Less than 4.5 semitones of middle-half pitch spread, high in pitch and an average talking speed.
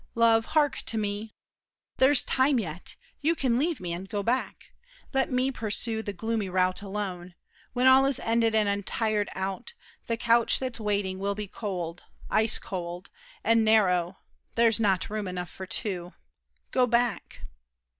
Yes: average, 3.8 semitones; high, 215 Hz; average, 155 wpm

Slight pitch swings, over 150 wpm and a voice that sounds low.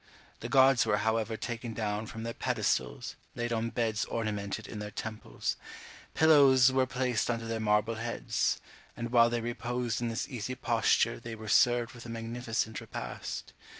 Yes: narrow, 1.6 semitones; average, 165 wpm; low, 115 Hz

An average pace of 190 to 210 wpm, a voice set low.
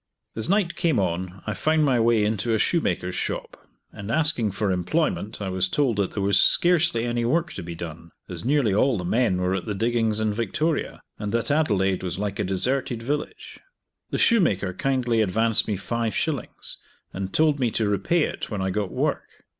Yes: average, 195 wpm; low, 110 Hz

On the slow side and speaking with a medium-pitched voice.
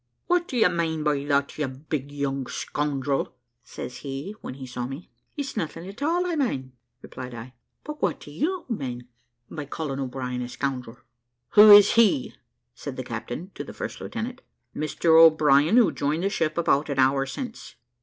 No: average, 185 wpm; medium, 150 Hz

